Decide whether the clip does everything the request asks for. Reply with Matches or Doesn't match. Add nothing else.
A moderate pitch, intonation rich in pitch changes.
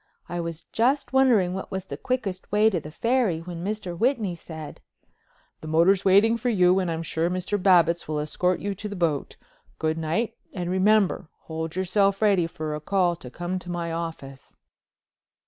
Doesn't match